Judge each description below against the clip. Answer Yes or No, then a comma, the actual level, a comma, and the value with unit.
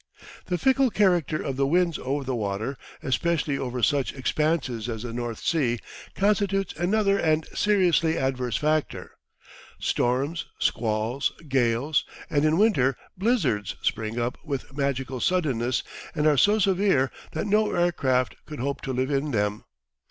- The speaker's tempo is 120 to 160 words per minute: Yes, average, 145 wpm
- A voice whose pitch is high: No, medium, 140 Hz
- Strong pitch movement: Yes, wide, 5.7 semitones